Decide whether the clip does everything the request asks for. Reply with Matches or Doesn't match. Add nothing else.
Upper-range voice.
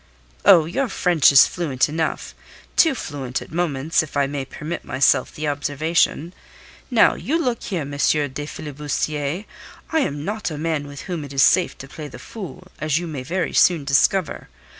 Doesn't match